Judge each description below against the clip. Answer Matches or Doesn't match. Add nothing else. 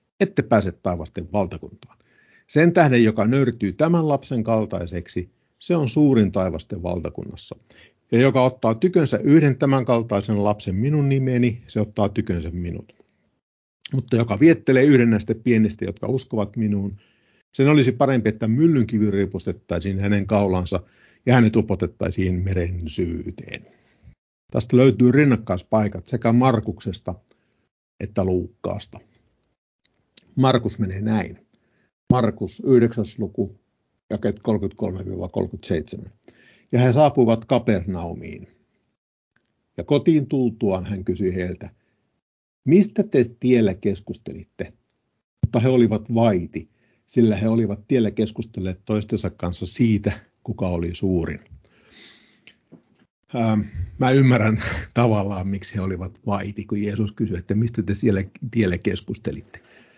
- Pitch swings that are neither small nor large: Matches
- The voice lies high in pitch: Doesn't match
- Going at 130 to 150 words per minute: Doesn't match